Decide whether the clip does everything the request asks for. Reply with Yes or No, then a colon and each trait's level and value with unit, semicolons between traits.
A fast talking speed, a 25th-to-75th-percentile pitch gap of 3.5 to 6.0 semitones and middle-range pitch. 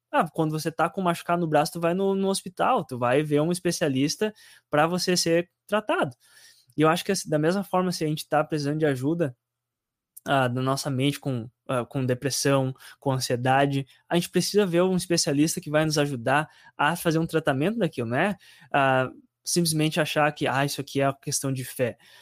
Yes: fast, 200 wpm; average, 4.0 semitones; medium, 150 Hz